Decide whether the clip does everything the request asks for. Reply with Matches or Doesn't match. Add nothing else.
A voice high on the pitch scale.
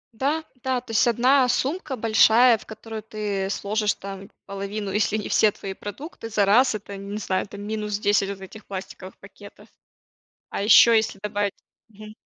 Matches